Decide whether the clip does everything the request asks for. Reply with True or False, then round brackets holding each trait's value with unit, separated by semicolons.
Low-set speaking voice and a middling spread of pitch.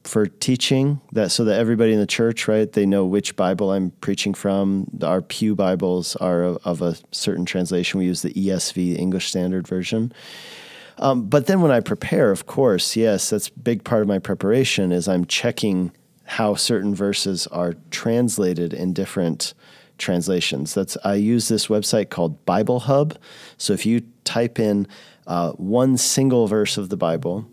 True (100 Hz; 4.1 semitones)